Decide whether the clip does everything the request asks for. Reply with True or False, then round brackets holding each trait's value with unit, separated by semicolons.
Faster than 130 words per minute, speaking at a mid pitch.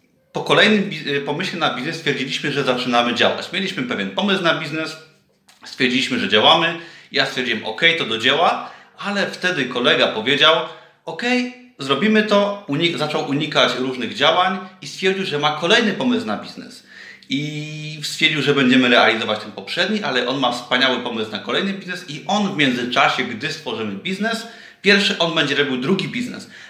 True (160 wpm; 155 Hz)